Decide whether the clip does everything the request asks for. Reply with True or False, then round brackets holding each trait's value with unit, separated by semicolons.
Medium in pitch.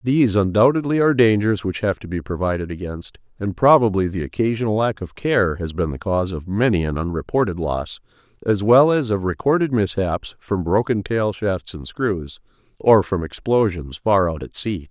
False (100 Hz)